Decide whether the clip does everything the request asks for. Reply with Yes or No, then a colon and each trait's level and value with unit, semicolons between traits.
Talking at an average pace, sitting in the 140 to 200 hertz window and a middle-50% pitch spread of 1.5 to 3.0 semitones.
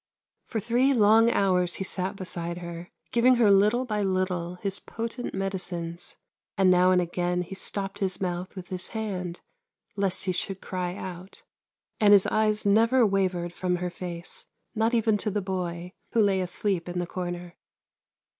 Yes: average, 165 wpm; high, 190 Hz; average, 2.7 semitones